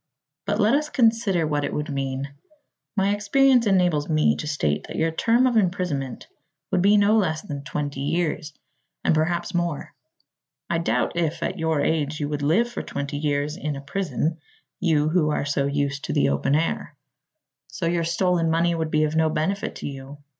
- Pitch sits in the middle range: Yes, medium, 160 Hz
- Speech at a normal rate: Yes, average, 190 wpm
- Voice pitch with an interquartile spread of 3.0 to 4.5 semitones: Yes, average, 3.9 semitones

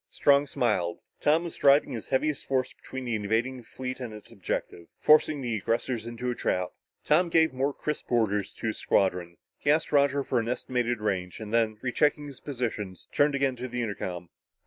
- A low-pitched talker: Yes, low, 125 Hz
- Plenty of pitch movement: No, average, 4.5 semitones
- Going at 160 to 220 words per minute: Yes, average, 190 wpm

